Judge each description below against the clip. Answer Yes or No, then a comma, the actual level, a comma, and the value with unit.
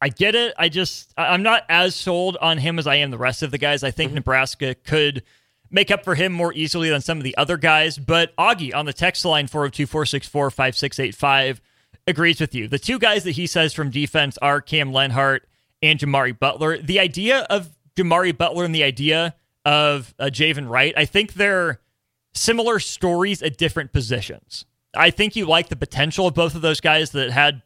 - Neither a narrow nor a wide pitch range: Yes, average, 3.7 semitones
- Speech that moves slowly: No, average, 195 wpm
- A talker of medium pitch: Yes, medium, 155 Hz